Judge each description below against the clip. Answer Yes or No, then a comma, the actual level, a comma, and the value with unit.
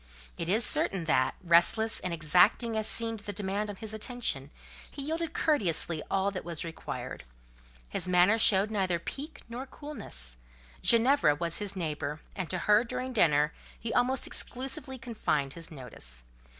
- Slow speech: No, average, 155 wpm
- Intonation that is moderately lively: No, wide, 6.0 semitones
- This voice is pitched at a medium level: No, high, 200 Hz